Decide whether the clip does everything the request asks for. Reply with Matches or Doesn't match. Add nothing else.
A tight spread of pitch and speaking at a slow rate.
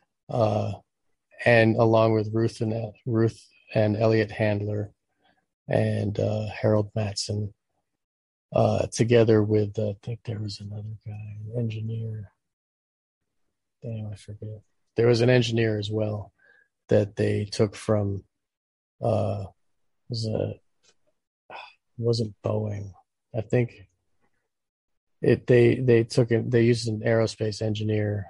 Matches